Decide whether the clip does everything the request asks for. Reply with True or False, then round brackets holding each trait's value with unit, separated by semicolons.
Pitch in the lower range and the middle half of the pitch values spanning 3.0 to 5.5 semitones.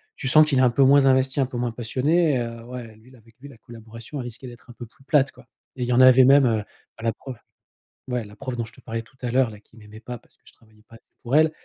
False (125 Hz; 2.6 semitones)